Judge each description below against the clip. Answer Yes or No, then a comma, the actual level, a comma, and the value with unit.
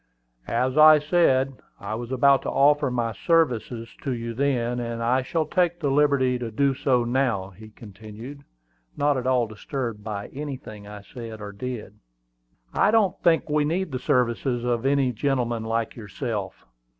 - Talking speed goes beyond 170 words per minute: No, average, 165 wpm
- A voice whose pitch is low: Yes, low, 125 Hz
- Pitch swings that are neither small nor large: Yes, average, 3.7 semitones